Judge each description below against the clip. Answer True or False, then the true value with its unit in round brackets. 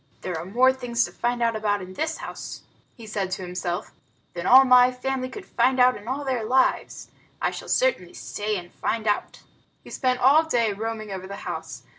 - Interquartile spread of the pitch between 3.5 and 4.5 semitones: True (4.2 semitones)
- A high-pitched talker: True (235 Hz)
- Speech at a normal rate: False (210 wpm)